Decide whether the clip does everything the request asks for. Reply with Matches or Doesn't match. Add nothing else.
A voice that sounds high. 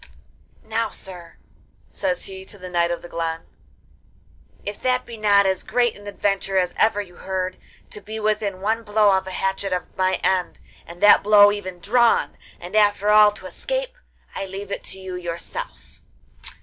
Matches